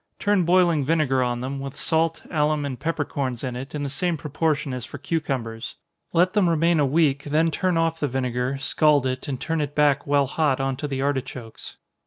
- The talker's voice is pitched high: No, medium, 145 Hz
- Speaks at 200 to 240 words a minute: Yes, fast, 205 wpm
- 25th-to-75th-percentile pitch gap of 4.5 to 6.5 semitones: No, average, 3.6 semitones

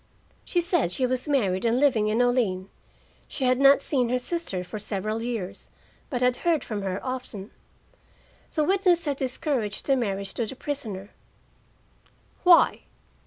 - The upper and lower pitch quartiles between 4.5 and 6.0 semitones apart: Yes, average, 5.1 semitones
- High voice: Yes, very high, 250 Hz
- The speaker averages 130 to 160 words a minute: Yes, average, 155 wpm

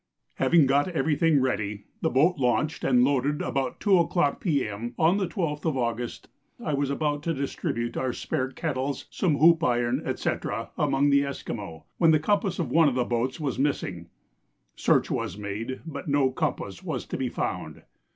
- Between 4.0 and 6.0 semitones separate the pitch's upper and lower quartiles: Yes, average, 4.3 semitones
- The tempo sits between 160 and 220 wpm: Yes, average, 180 wpm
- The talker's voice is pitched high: No, medium, 140 Hz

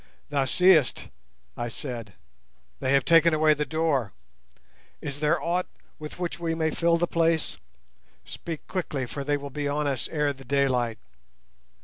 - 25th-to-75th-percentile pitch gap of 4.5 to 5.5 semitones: No, average, 3.3 semitones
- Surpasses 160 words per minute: No, average, 155 wpm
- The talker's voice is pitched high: No, medium, 150 Hz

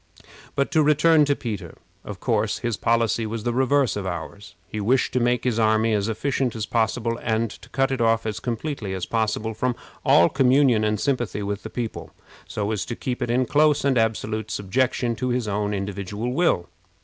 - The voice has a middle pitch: No, low, 115 Hz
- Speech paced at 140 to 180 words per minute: No, average, 195 wpm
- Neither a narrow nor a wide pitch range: Yes, average, 3.1 semitones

